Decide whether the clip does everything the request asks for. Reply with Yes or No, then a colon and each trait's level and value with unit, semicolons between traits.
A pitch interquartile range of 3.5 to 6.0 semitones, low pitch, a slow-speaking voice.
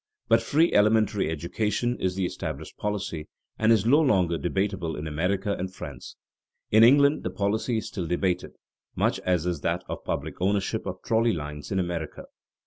No: average, 4.0 semitones; very low, 95 Hz; average, 170 wpm